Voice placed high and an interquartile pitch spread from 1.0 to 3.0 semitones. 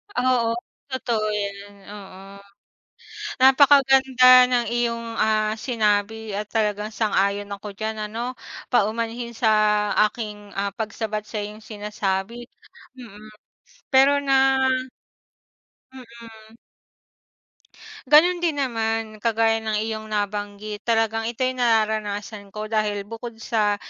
Yes: high, 220 Hz; narrow, 2.5 semitones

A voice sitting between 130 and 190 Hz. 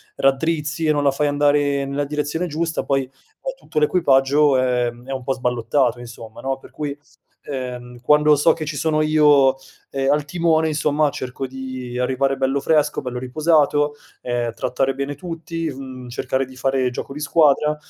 Yes: medium, 140 Hz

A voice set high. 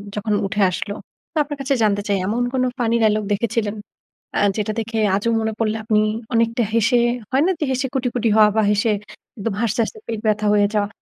Yes: high, 220 Hz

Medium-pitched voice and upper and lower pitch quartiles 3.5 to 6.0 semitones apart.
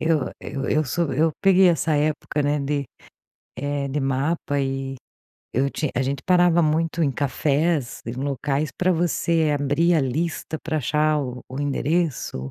No: medium, 145 Hz; average, 3.0 semitones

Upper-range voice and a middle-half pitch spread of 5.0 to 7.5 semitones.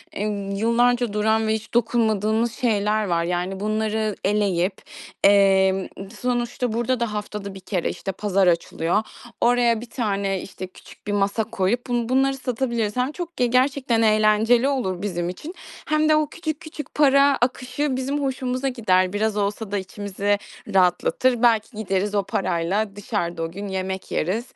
No: high, 215 Hz; average, 3.9 semitones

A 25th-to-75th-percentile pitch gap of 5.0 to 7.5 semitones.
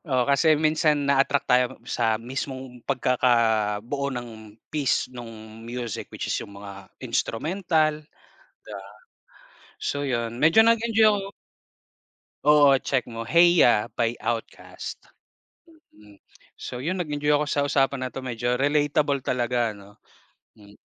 No: average, 4.3 semitones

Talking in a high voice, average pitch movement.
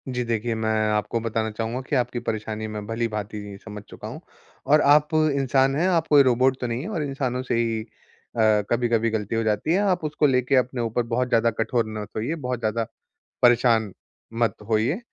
No: low, 120 Hz; average, 3.2 semitones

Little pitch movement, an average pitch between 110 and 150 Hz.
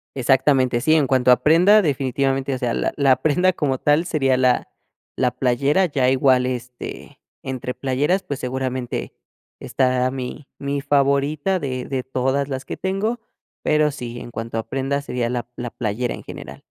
Yes: narrow, 2.3 semitones; low, 135 Hz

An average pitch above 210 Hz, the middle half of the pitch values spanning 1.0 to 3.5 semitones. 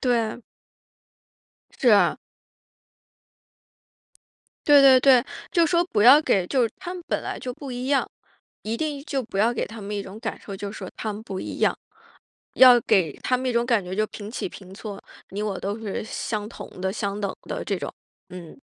No: high, 225 Hz; average, 4.3 semitones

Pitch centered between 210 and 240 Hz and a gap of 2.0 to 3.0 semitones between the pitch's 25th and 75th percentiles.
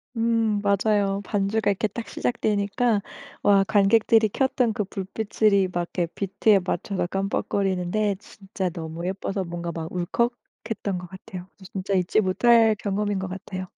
No: high, 200 Hz; narrow, 2.5 semitones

